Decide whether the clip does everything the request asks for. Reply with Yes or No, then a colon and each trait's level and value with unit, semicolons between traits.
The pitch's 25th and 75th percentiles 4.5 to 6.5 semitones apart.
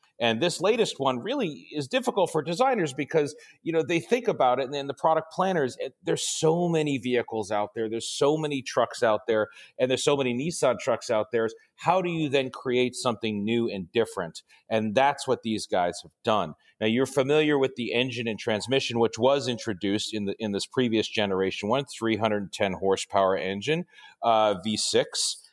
Yes: average, 5.2 semitones